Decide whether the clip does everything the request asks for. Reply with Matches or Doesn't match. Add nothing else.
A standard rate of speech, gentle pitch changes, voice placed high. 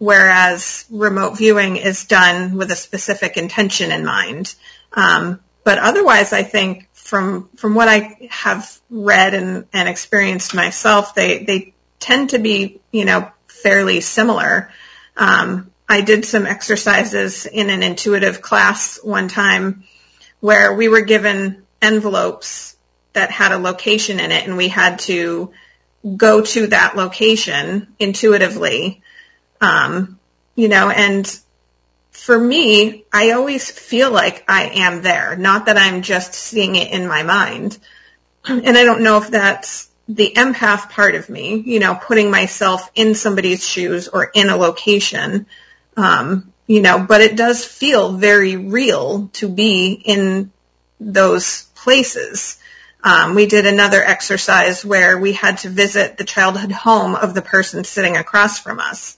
Matches